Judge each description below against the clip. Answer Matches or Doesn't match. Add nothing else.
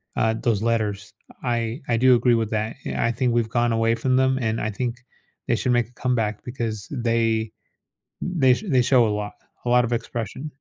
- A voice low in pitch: Matches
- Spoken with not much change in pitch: Matches